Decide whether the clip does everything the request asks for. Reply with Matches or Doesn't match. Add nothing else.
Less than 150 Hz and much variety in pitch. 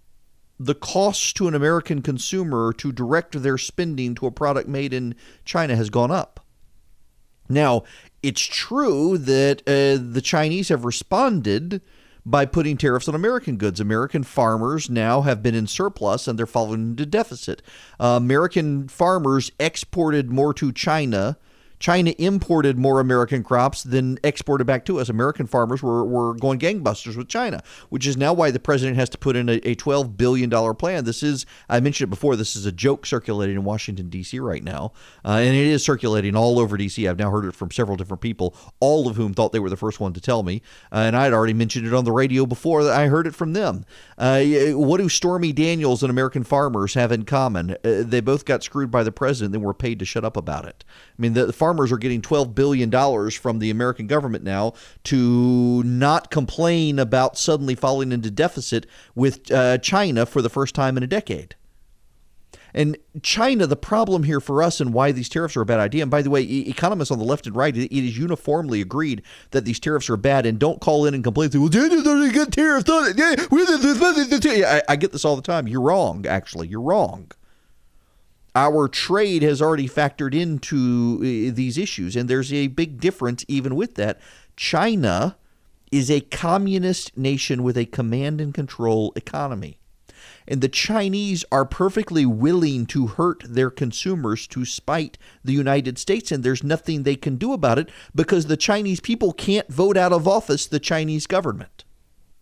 Doesn't match